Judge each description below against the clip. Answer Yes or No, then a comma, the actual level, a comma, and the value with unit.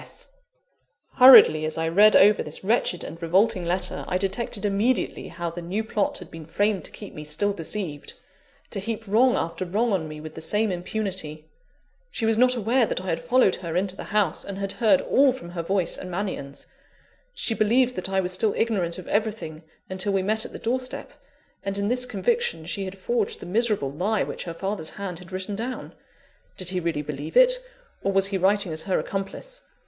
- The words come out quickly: Yes, fast, 210 wpm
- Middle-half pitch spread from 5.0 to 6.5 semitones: No, average, 4.2 semitones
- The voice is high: Yes, high, 195 Hz